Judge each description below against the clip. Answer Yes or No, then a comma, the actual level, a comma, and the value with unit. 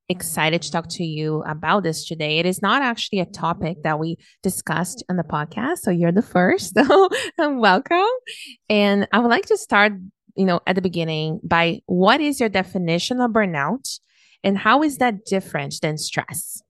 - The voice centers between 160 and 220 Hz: Yes, high, 190 Hz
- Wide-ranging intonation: Yes, wide, 5.7 semitones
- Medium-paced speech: Yes, average, 185 wpm